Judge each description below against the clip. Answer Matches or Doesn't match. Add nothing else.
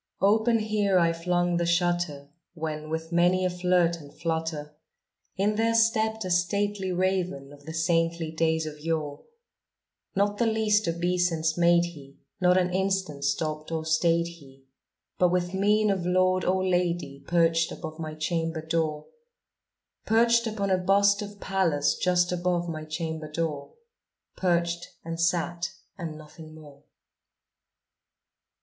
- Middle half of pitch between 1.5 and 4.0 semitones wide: Matches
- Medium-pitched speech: Matches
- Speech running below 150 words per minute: Matches